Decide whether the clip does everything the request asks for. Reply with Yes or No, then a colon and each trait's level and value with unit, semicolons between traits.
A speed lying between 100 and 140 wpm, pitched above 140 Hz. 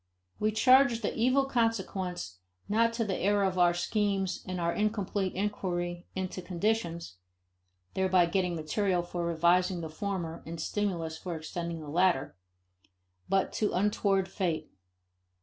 Yes: slow, 135 wpm; medium, 185 Hz